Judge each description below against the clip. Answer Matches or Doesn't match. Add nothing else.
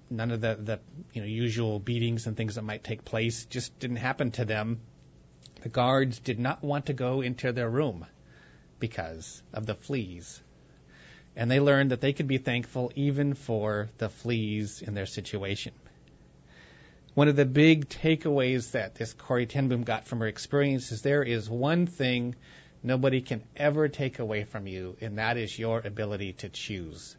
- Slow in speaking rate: Doesn't match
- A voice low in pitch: Matches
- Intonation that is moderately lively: Matches